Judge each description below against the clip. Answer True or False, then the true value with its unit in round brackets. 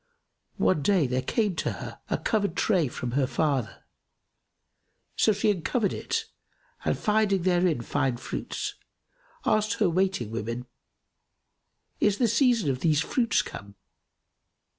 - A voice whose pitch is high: False (180 Hz)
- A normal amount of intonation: False (8.1 semitones)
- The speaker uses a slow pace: True (130 wpm)